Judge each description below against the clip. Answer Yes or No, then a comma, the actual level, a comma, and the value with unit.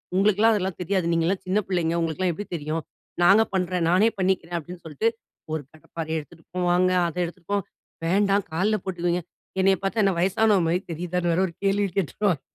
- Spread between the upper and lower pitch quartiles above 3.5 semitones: No, average, 2.7 semitones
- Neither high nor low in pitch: Yes, medium, 180 Hz